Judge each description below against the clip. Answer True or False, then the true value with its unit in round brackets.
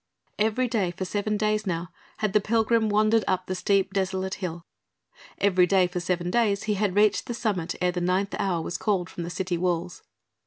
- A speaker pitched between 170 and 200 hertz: True (190 Hz)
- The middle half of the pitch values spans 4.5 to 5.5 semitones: False (3.0 semitones)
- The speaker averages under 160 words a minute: False (200 wpm)